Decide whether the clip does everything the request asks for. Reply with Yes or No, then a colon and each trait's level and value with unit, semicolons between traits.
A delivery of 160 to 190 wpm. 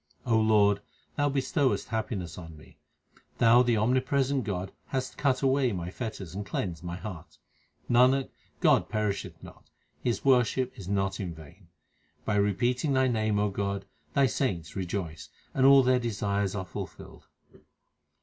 No: average, 145 wpm